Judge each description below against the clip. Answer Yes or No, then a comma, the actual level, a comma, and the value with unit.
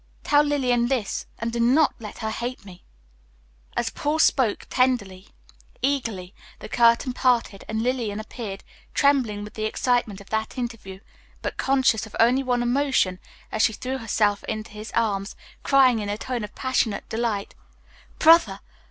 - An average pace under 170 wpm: Yes, average, 155 wpm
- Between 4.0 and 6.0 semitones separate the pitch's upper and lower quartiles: No, average, 3.5 semitones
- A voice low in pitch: No, high, 230 Hz